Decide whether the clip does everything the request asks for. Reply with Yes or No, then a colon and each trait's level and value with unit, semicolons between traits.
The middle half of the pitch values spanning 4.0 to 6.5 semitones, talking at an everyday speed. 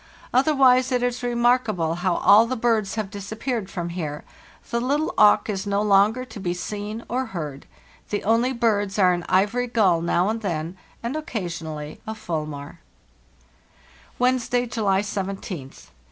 Yes: average, 4.9 semitones; average, 150 wpm